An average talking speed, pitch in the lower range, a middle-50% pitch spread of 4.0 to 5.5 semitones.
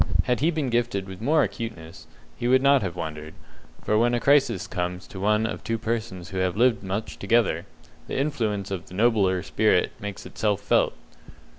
Yes: average, 185 wpm; low, 105 Hz; average, 4.3 semitones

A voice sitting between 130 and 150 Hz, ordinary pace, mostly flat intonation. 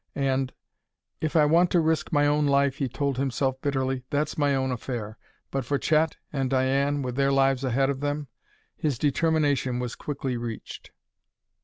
Yes: low, 135 Hz; average, 175 wpm; narrow, 1.8 semitones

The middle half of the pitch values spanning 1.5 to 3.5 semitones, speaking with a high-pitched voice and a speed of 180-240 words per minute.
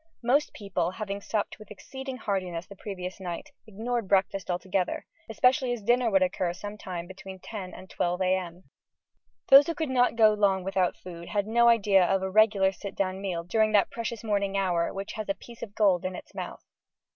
Yes: average, 3.0 semitones; high, 195 Hz; average, 195 wpm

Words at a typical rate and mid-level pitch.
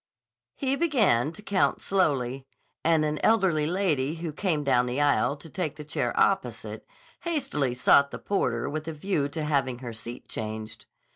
Yes: average, 165 wpm; medium, 150 Hz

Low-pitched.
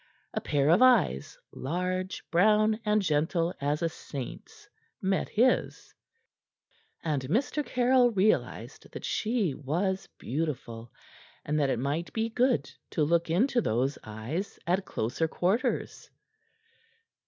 No: medium, 175 Hz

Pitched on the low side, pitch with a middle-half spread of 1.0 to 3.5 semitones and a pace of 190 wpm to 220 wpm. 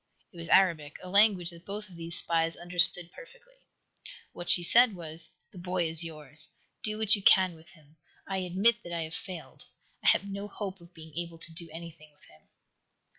No: medium, 175 Hz; average, 3.0 semitones; average, 200 wpm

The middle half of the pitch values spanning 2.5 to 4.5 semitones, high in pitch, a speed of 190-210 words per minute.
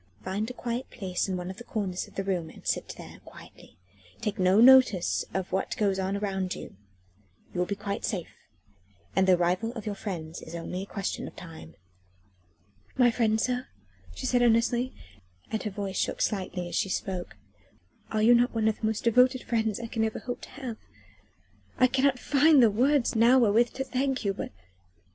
Yes: average, 4.2 semitones; high, 215 Hz; average, 195 wpm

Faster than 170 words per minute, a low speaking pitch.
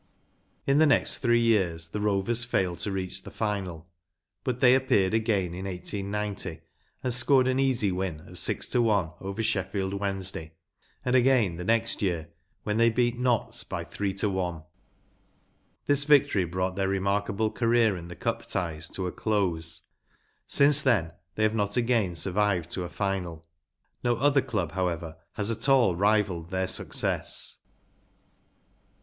No: average, 165 wpm; low, 100 Hz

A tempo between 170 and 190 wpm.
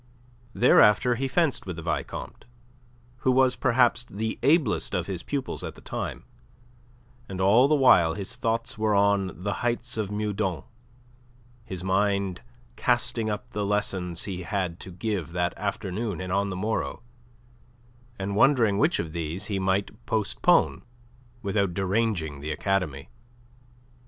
No: average, 140 wpm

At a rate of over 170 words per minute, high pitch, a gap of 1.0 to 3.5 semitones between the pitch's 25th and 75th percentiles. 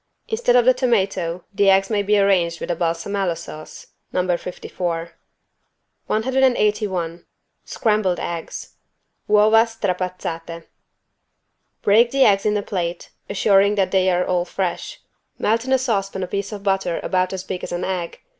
No: average, 155 wpm; high, 195 Hz; average, 3.0 semitones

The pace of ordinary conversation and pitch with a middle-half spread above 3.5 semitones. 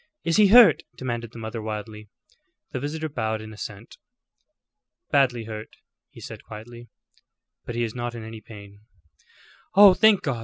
Yes: average, 155 wpm; average, 4.0 semitones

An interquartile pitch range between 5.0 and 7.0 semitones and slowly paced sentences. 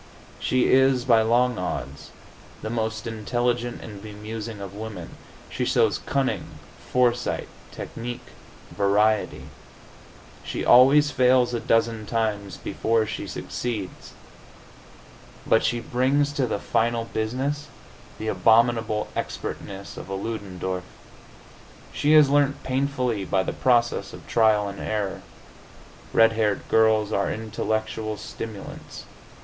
No: narrow, 2.6 semitones; slow, 115 wpm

